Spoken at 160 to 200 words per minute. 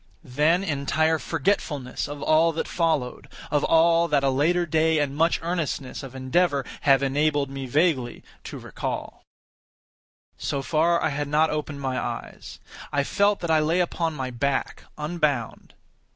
No: average, 150 wpm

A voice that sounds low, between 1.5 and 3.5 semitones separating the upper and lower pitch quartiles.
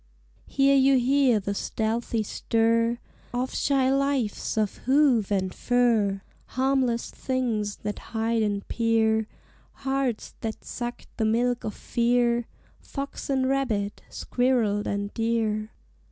No: high, 235 Hz; average, 3.2 semitones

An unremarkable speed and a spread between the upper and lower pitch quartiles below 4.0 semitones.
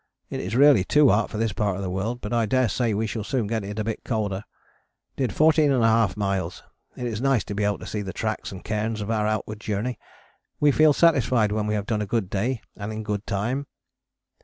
No: fast, 230 wpm; average, 2.9 semitones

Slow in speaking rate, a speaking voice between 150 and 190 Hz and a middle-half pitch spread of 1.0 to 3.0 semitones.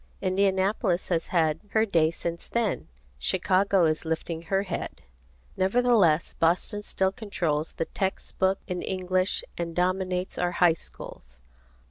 Yes: slow, 130 wpm; medium, 185 Hz; narrow, 2.6 semitones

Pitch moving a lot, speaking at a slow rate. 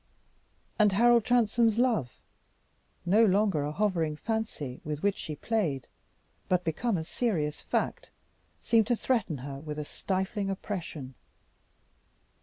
Yes: wide, 6.6 semitones; slow, 125 wpm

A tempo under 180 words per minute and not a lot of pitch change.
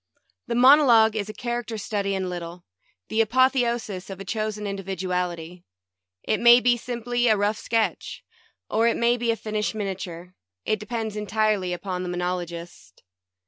No: average, 160 wpm; average, 4.2 semitones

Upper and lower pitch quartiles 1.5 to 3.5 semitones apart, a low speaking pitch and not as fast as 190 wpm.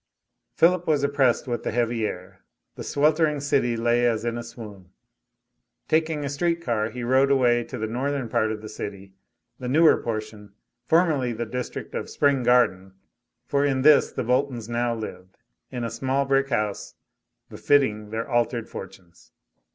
No: average, 4.2 semitones; low, 120 Hz; average, 165 wpm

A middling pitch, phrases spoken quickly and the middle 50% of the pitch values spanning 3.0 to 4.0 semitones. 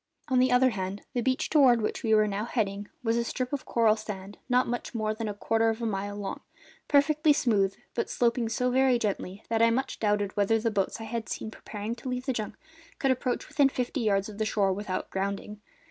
No: high, 225 Hz; fast, 225 wpm; average, 3.4 semitones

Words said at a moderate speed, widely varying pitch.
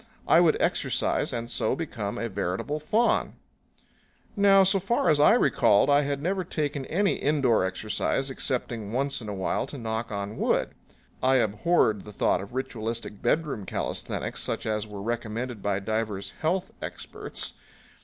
Yes: average, 155 wpm; wide, 5.8 semitones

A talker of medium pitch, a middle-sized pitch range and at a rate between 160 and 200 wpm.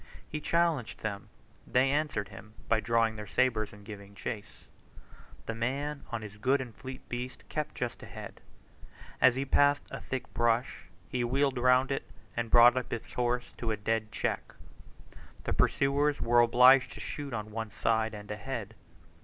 No: low, 120 Hz; average, 3.4 semitones; average, 170 wpm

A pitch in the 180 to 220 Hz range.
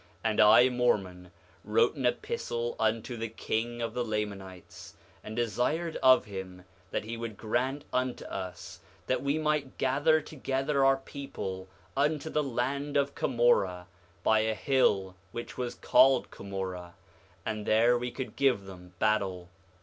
No: low, 120 Hz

